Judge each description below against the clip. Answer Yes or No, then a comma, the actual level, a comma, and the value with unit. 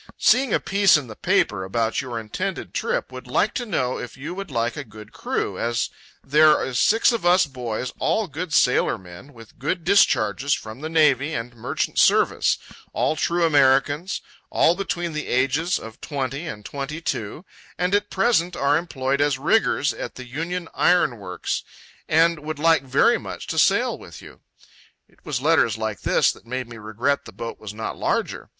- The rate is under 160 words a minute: No, average, 180 wpm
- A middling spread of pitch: No, wide, 5.9 semitones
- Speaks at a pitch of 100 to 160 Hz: Yes, medium, 140 Hz